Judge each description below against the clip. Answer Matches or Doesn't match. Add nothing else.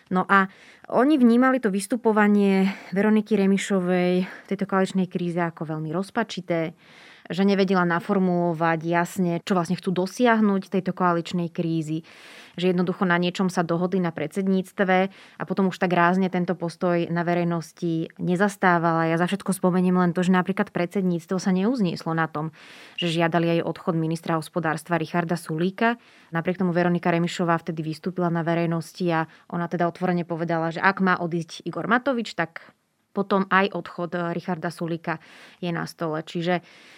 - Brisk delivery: Doesn't match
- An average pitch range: Doesn't match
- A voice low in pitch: Doesn't match